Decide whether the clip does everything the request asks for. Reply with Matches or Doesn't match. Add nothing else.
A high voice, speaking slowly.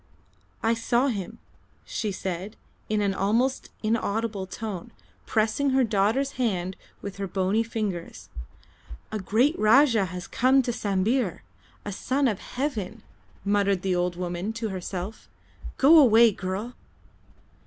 Matches